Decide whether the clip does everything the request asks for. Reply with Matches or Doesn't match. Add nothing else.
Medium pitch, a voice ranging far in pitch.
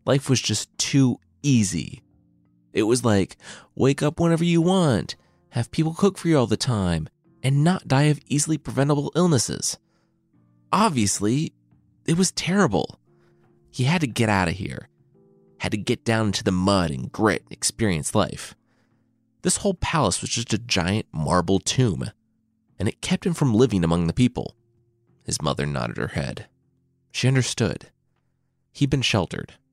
Doesn't match